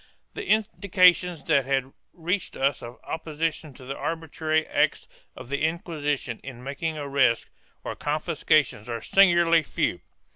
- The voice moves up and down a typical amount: Yes, average, 3.5 semitones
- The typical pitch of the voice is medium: Yes, medium, 155 Hz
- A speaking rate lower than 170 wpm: Yes, slow, 135 wpm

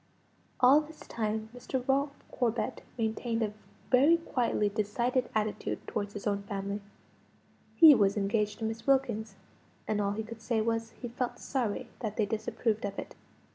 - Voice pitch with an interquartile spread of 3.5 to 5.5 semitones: No, average, 3.0 semitones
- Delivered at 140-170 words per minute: Yes, average, 160 wpm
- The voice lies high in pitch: Yes, high, 225 Hz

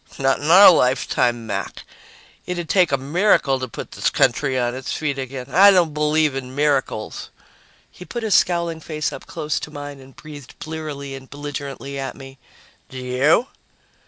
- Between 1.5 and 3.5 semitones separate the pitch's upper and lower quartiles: Yes, average, 3.0 semitones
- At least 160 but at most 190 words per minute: Yes, average, 170 wpm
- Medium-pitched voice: Yes, medium, 145 Hz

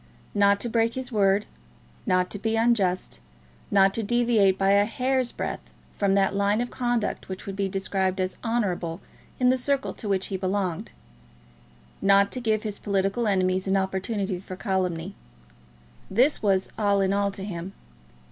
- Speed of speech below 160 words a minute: No, average, 165 wpm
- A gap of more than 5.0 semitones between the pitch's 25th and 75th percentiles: No, average, 2.8 semitones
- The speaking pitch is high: Yes, high, 200 Hz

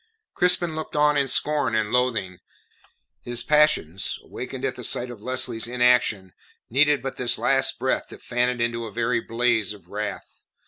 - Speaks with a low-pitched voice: Yes, low, 120 Hz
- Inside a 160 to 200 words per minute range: Yes, average, 170 wpm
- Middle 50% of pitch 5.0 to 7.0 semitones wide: No, average, 3.2 semitones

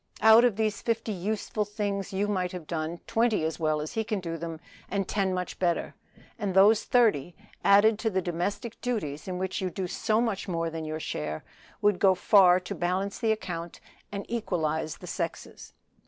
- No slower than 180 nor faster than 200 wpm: Yes, average, 185 wpm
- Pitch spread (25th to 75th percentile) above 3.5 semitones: Yes, average, 4.0 semitones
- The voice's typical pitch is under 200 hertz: Yes, high, 190 Hz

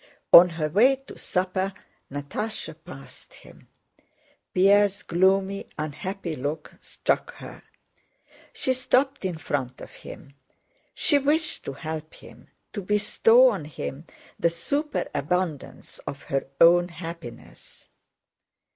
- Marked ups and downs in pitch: No, average, 5.0 semitones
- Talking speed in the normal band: No, slow, 110 wpm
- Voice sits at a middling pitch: Yes, medium, 180 Hz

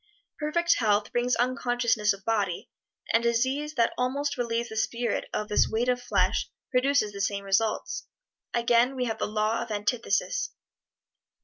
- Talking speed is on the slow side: No, average, 150 wpm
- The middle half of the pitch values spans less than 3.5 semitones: Yes, average, 2.8 semitones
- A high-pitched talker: Yes, high, 235 Hz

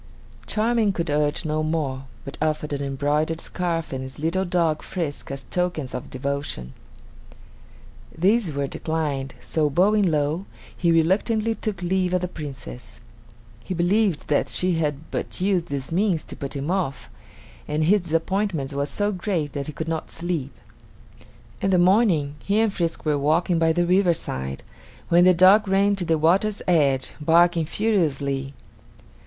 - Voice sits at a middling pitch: Yes, medium, 165 Hz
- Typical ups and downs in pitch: Yes, average, 4.2 semitones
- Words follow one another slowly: No, average, 160 wpm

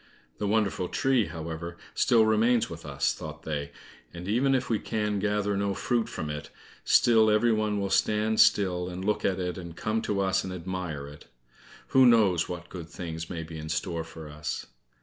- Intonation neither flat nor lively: Yes, average, 4.6 semitones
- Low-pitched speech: Yes, very low, 95 Hz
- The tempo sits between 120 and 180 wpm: No, average, 190 wpm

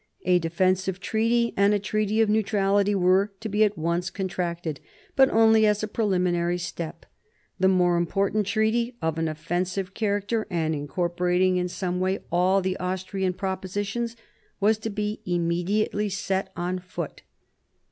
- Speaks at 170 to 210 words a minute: No, average, 145 wpm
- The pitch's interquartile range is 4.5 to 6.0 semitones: No, average, 2.8 semitones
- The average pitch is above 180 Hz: Yes, high, 190 Hz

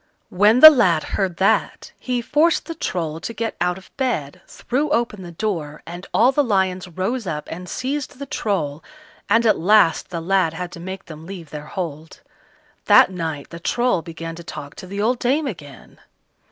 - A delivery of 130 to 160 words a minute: No, average, 190 wpm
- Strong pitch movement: Yes, wide, 6.2 semitones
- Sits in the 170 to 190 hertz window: Yes, medium, 185 Hz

